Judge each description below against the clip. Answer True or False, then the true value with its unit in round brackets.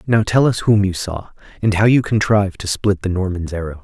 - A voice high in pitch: False (100 Hz)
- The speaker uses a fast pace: True (235 wpm)